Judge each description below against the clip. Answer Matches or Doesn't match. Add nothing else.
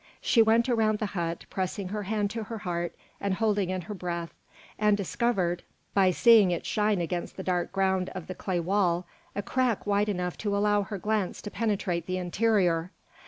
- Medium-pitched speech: Doesn't match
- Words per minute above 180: Matches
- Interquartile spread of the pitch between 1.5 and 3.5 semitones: Matches